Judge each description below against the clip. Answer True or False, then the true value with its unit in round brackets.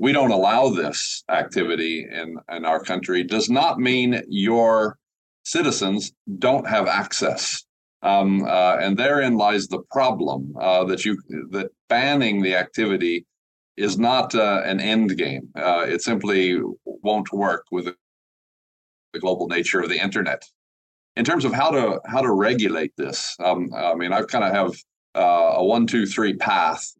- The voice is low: True (95 Hz)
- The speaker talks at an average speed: True (160 wpm)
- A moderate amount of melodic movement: True (3.8 semitones)